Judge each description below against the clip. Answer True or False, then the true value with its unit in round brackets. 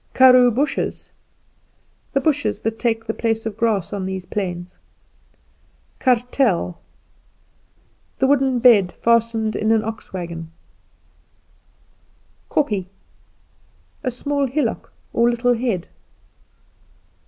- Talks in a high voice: True (230 Hz)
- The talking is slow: True (110 wpm)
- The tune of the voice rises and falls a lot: False (3.7 semitones)